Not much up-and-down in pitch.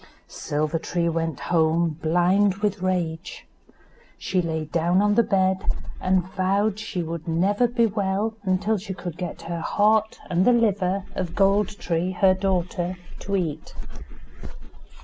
No: average, 3.1 semitones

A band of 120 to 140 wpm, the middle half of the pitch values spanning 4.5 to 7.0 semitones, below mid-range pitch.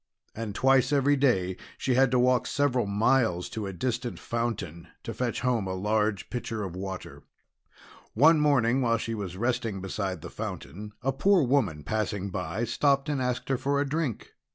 No: average, 175 wpm; average, 5.1 semitones; low, 115 Hz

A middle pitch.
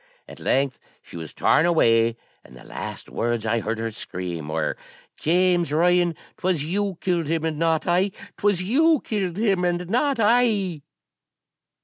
Yes: medium, 175 Hz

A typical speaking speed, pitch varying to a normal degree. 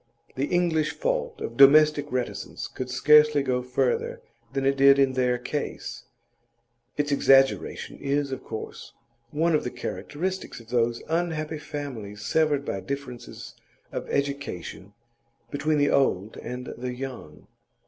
No: slow, 130 wpm; average, 3.3 semitones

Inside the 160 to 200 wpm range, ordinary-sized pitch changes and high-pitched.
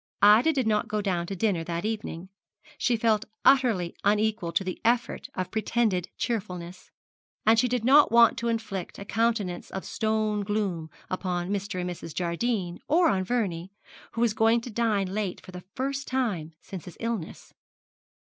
Yes: average, 170 wpm; average, 4.1 semitones; high, 210 Hz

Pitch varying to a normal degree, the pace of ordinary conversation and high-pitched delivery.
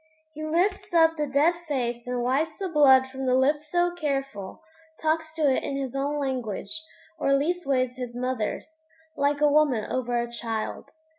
Yes: average, 3.6 semitones; average, 170 wpm; very high, 275 Hz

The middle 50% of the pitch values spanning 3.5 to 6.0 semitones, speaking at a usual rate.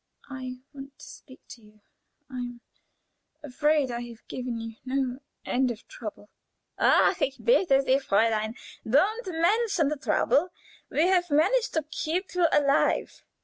Yes: wide, 5.5 semitones; average, 145 wpm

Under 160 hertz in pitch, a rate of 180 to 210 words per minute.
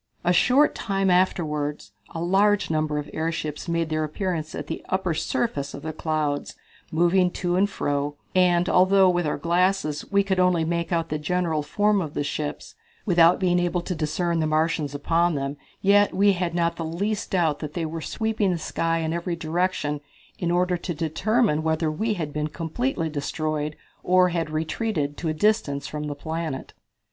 No: medium, 170 Hz; average, 185 wpm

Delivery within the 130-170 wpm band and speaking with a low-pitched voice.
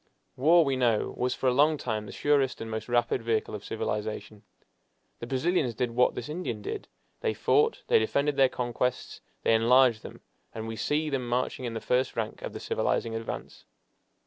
No: average, 190 wpm; low, 125 Hz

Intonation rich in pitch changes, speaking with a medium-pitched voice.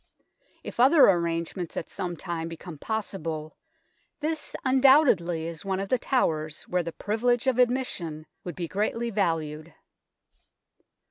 Yes: wide, 6.6 semitones; medium, 180 Hz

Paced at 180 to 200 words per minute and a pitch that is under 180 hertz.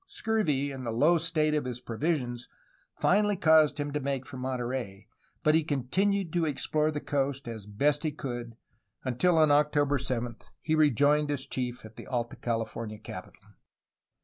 No: average, 165 wpm; medium, 140 Hz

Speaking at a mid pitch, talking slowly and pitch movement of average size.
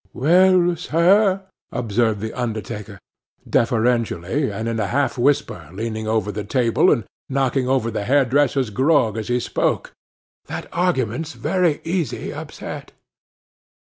No: low, 125 Hz; slow, 125 wpm; average, 4.9 semitones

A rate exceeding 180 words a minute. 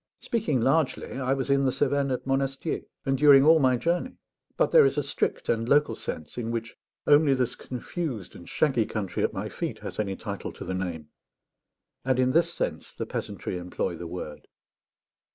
Yes: average, 190 wpm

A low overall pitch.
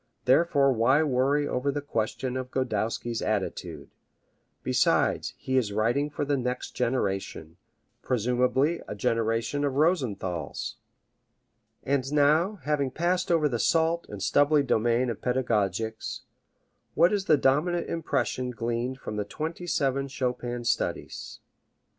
Yes: low, 130 Hz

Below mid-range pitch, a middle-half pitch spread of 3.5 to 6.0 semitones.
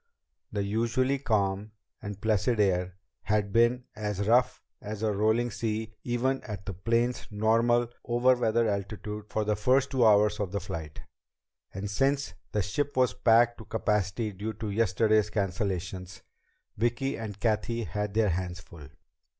No: low, 105 Hz; average, 2.8 semitones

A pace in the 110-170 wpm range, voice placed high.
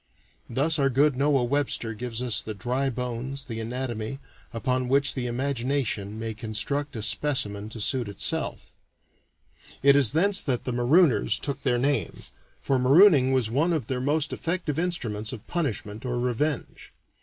No: average, 155 wpm; low, 130 Hz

